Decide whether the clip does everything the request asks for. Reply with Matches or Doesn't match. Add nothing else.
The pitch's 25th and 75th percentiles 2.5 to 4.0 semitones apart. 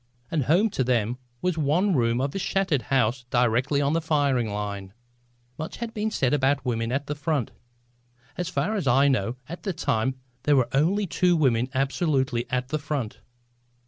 Doesn't match